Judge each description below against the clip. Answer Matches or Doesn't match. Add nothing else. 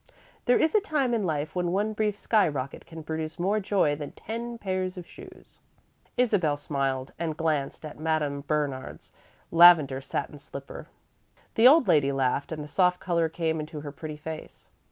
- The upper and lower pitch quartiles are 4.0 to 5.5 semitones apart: Matches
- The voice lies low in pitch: Doesn't match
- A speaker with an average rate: Matches